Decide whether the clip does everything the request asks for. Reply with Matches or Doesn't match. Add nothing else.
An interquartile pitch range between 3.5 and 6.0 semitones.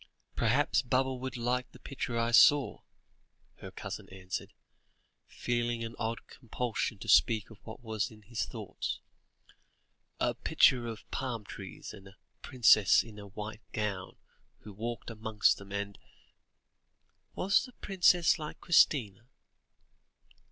Doesn't match